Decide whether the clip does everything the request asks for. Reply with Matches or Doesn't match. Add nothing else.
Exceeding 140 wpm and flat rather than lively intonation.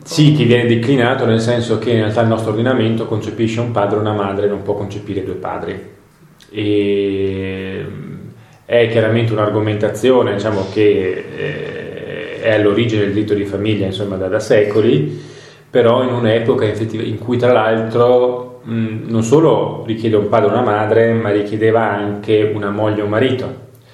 Doesn't match